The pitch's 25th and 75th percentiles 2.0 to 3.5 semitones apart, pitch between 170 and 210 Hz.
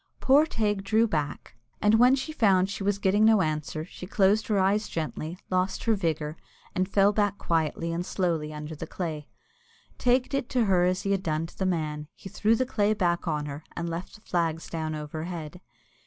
No: average, 4.6 semitones; medium, 185 Hz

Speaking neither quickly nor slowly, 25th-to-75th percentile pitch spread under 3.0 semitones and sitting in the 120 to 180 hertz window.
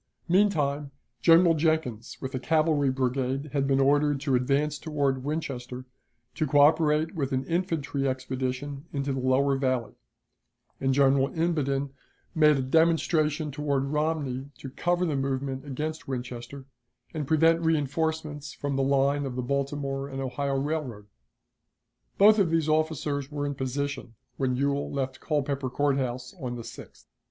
Yes: average, 145 wpm; narrow, 2.4 semitones; medium, 140 Hz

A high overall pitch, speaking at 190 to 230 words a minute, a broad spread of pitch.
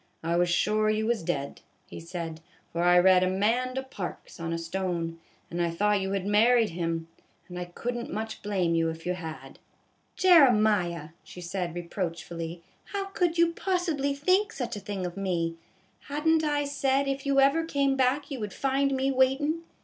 Yes: high, 210 Hz; average, 195 wpm; wide, 7.8 semitones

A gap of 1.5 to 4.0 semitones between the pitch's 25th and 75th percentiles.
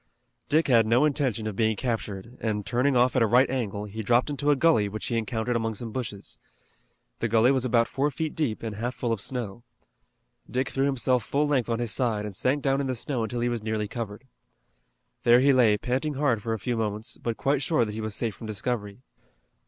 Yes: average, 3.1 semitones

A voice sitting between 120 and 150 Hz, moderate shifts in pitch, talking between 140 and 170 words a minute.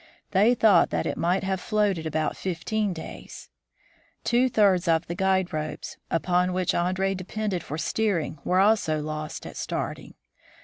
No: medium, 185 Hz; average, 3.5 semitones; average, 150 wpm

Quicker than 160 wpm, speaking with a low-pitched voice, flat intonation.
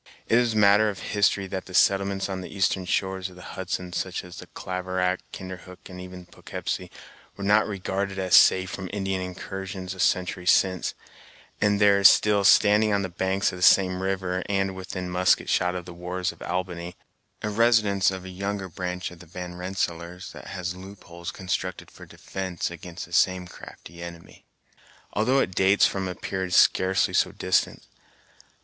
Yes: average, 175 wpm; very low, 95 Hz; narrow, 1.4 semitones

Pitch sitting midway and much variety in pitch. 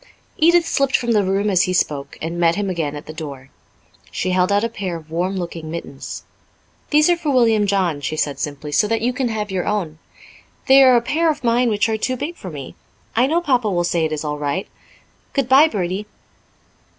No: high, 200 Hz; wide, 6.9 semitones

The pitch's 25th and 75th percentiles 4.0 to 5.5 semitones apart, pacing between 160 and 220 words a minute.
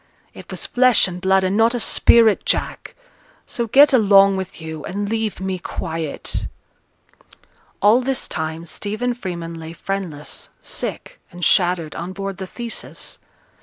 No: average, 4.6 semitones; average, 145 wpm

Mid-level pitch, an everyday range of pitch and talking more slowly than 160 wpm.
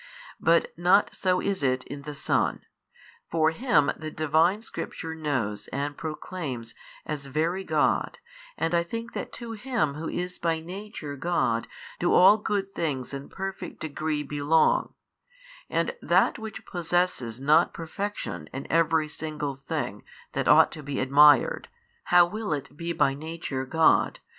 Yes: medium, 160 Hz; average, 3.8 semitones; average, 150 wpm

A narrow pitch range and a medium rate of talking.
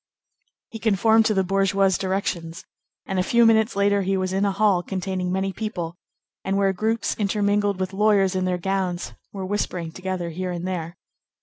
Yes: narrow, 1.8 semitones; average, 180 wpm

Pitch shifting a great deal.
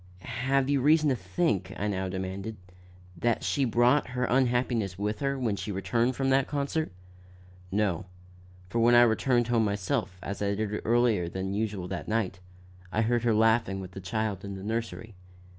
No: average, 3.8 semitones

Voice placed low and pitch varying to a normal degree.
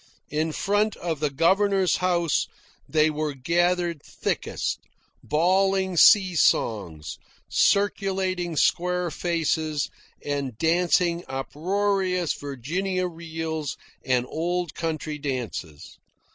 No: medium, 170 Hz; average, 3.5 semitones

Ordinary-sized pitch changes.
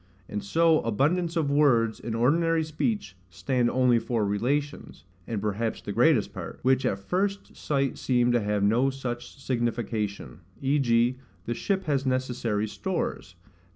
Yes: average, 4.3 semitones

